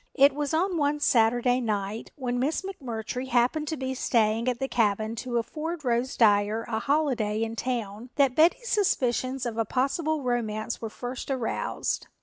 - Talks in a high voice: Yes, high, 245 Hz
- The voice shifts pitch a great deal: No, average, 3.9 semitones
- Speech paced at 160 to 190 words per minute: Yes, average, 165 wpm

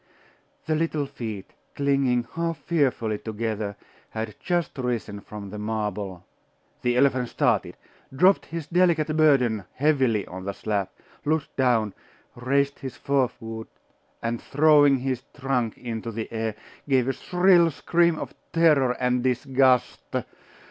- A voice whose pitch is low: Yes, low, 125 Hz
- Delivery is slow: Yes, slow, 125 wpm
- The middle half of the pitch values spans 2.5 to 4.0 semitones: No, average, 4.6 semitones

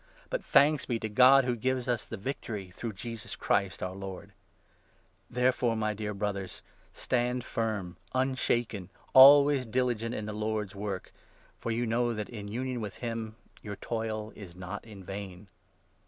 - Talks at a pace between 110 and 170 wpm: Yes, average, 165 wpm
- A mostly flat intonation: No, average, 3.3 semitones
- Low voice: Yes, low, 110 Hz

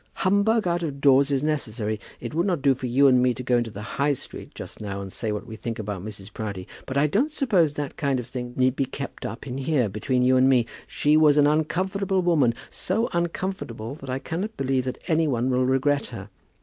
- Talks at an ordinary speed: No, fast, 235 wpm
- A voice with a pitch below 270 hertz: Yes, low, 135 Hz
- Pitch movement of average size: Yes, average, 4.5 semitones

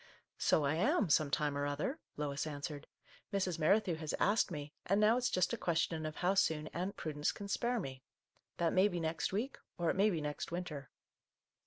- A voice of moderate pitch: Yes, medium, 165 Hz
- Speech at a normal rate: No, fast, 215 wpm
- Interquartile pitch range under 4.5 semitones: No, average, 4.8 semitones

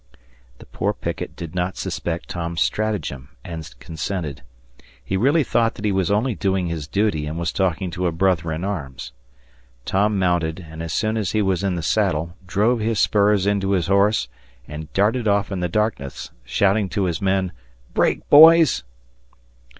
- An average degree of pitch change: Yes, average, 3.8 semitones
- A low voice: Yes, very low, 95 Hz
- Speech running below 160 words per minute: No, average, 175 wpm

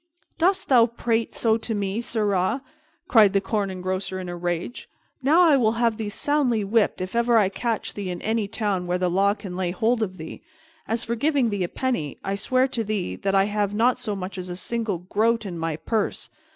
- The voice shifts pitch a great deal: No, average, 3.9 semitones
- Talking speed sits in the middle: No, fast, 220 wpm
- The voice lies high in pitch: Yes, high, 210 Hz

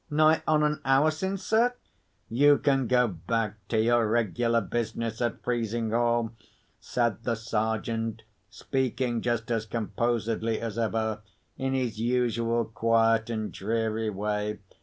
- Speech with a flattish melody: Yes, narrow, 1.9 semitones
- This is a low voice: Yes, low, 115 Hz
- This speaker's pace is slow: Yes, slow, 130 wpm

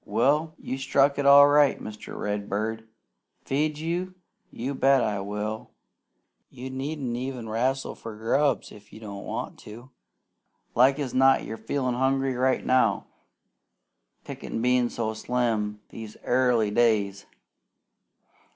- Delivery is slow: Yes, slow, 130 wpm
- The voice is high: No, low, 125 Hz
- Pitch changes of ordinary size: Yes, average, 3.7 semitones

